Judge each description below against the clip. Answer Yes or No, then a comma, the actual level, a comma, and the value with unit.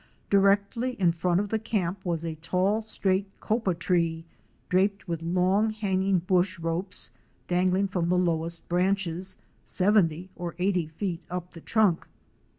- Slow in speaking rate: No, average, 145 wpm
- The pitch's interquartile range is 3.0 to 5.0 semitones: No, narrow, 2.6 semitones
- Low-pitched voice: No, medium, 185 Hz